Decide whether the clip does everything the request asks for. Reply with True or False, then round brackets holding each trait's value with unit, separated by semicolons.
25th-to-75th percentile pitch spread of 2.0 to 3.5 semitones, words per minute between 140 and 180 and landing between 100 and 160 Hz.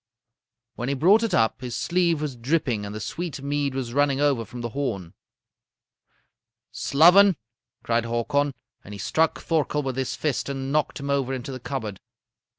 False (3.9 semitones; 170 wpm; 135 Hz)